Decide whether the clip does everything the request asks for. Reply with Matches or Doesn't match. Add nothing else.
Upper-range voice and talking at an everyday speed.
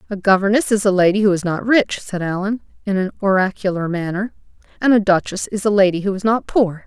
Doesn't match